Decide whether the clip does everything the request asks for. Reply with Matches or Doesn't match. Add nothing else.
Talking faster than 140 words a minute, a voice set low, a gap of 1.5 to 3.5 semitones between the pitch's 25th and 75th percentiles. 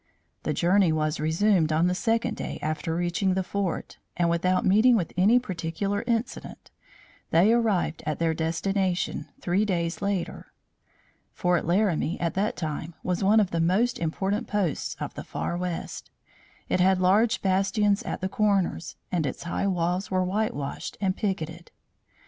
Doesn't match